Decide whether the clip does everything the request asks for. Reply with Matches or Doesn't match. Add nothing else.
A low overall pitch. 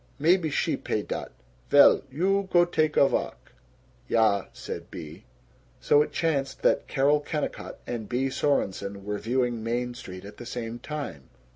Matches